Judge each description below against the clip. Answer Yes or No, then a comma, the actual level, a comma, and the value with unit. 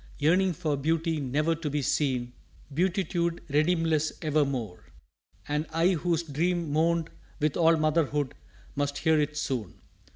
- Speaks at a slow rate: Yes, slow, 130 wpm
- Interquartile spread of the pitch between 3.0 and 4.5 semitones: No, narrow, 2.5 semitones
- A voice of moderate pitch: Yes, medium, 155 Hz